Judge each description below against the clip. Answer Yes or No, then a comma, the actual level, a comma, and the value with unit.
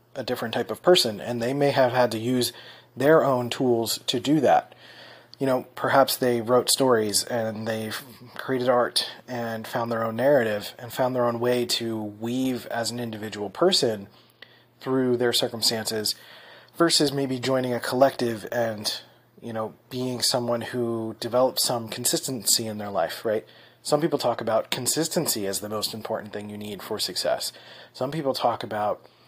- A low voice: Yes, low, 120 Hz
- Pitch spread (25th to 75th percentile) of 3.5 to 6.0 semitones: No, narrow, 2.5 semitones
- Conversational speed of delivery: Yes, average, 170 wpm